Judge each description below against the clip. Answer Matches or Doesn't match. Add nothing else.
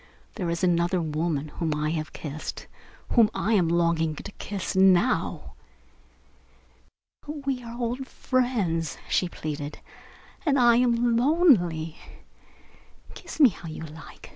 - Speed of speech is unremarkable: Doesn't match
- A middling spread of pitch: Doesn't match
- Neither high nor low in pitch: Matches